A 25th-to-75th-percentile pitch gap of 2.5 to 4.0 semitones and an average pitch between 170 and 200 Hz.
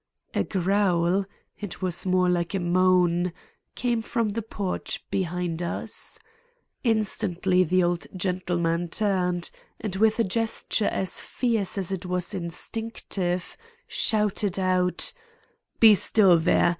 Yes: average, 2.8 semitones; medium, 185 Hz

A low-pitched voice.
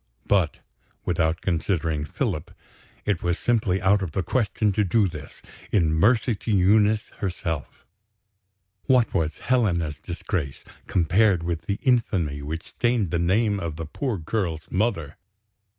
Yes: very low, 90 Hz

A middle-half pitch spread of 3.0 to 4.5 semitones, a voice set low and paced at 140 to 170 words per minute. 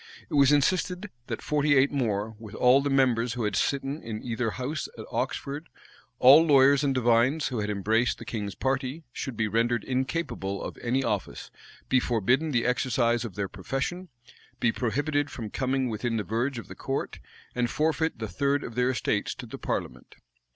No: average, 3.6 semitones; low, 125 Hz; average, 185 wpm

